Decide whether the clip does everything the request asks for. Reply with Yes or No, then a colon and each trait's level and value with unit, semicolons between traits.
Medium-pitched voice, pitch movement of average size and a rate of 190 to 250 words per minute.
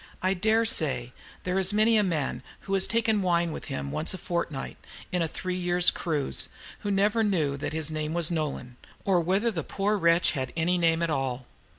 Yes: medium, 175 Hz; average, 3.9 semitones; fast, 205 wpm